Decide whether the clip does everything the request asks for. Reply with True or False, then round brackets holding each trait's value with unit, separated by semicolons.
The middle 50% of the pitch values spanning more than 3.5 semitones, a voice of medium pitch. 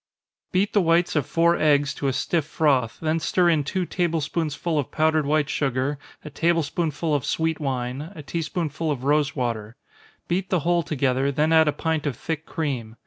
False (2.9 semitones; 155 Hz)